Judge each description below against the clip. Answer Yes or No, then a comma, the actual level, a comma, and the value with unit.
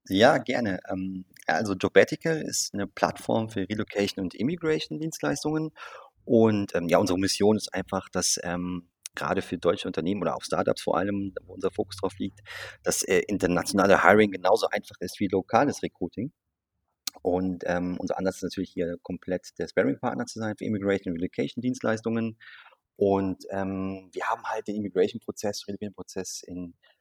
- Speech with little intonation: No, average, 3.0 semitones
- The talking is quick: No, average, 155 wpm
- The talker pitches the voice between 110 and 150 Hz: No, low, 100 Hz